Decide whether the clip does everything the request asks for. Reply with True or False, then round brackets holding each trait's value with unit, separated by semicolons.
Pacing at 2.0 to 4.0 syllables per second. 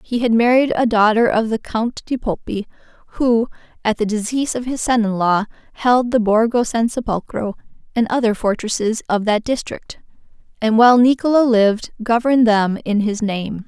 False (5.1 syllables/s)